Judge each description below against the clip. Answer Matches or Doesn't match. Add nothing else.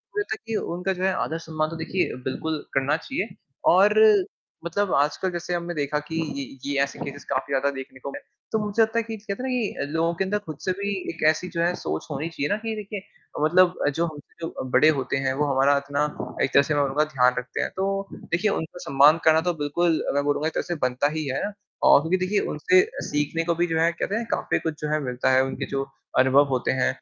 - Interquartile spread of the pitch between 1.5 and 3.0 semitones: Doesn't match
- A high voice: Doesn't match